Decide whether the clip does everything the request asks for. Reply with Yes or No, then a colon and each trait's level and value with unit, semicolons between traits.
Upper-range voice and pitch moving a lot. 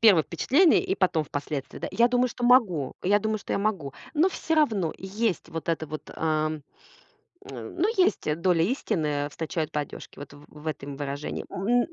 No: medium, 170 Hz; wide, 7.2 semitones